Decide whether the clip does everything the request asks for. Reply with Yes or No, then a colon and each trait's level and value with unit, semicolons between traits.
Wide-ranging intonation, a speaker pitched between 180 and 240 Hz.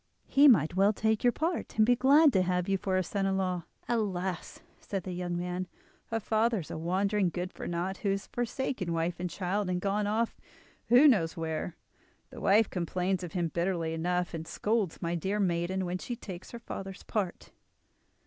No: average, 3.4 semitones; high, 190 Hz